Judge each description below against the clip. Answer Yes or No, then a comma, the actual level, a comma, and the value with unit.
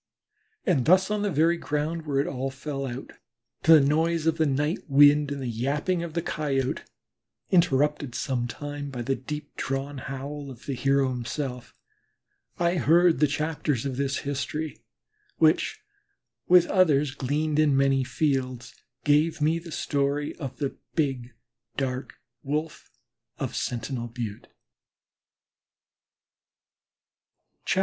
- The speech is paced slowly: Yes, slow, 130 wpm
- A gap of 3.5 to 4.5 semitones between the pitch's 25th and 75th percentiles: No, average, 2.8 semitones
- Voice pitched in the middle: Yes, medium, 145 Hz